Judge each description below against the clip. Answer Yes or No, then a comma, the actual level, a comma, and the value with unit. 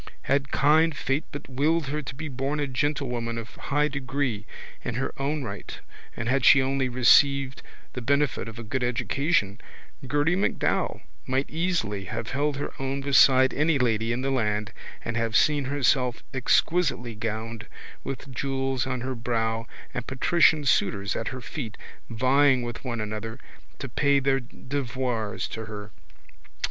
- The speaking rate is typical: Yes, average, 155 wpm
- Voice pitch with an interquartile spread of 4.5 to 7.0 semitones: No, average, 3.4 semitones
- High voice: No, low, 130 Hz